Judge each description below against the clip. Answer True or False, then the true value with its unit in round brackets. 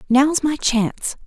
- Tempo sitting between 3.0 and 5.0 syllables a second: True (4.0 syllables/s)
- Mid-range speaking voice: False (265 Hz)